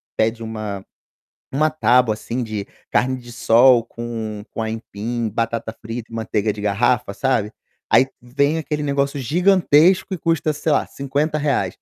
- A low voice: Yes, low, 120 Hz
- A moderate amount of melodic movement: Yes, average, 4.5 semitones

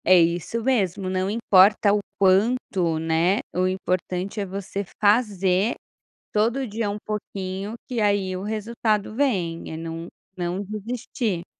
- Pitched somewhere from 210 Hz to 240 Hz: No, high, 195 Hz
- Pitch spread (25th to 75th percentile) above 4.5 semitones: No, average, 2.8 semitones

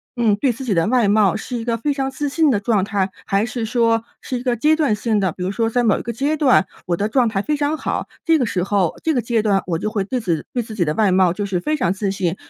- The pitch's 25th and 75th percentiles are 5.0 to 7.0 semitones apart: No, average, 4.3 semitones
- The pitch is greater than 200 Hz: Yes, high, 220 Hz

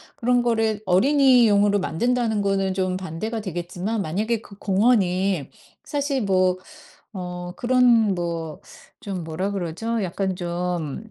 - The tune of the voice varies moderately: Yes, average, 4.1 semitones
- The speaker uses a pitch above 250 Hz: No, high, 195 Hz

